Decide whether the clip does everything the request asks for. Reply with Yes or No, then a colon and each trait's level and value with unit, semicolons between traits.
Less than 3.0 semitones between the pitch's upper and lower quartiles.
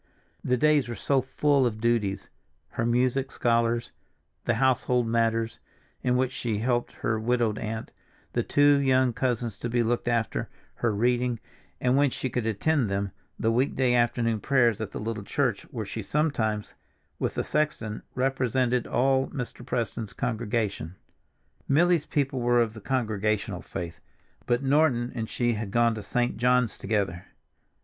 Yes: narrow, 2.6 semitones